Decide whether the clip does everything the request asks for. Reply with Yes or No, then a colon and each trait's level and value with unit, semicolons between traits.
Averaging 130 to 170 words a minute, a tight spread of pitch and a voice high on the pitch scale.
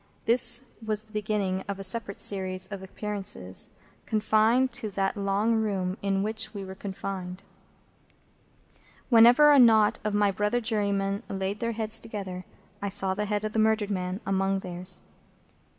Yes: average, 155 wpm; narrow, 2.2 semitones; high, 205 Hz